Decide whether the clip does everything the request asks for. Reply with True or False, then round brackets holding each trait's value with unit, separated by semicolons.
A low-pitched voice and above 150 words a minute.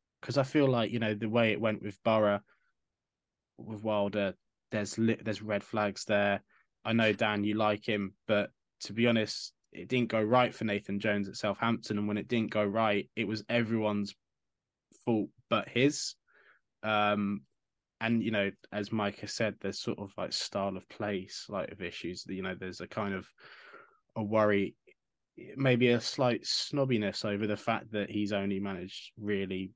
True (105 Hz; 180 wpm)